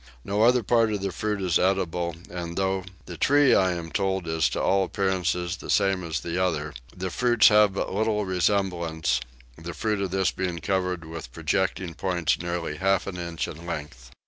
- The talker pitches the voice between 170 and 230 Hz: No, very low, 90 Hz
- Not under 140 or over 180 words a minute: No, average, 190 wpm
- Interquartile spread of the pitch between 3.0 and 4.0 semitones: No, narrow, 2.5 semitones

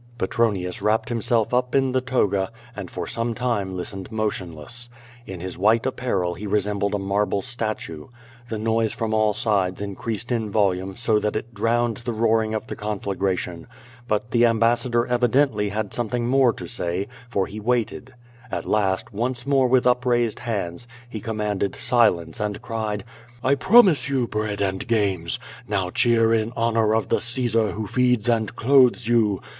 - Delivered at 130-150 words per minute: No, average, 170 wpm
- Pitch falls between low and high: No, low, 110 Hz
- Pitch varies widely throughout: No, average, 3.1 semitones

